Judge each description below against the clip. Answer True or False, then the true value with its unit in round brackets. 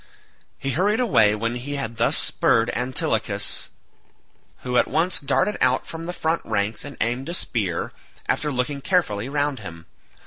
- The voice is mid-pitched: False (130 Hz)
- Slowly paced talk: False (160 wpm)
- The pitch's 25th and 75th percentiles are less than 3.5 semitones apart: False (5.5 semitones)